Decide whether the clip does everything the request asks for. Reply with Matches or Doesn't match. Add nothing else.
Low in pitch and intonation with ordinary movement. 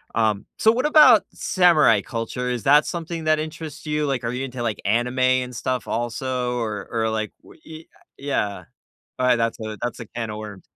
Matches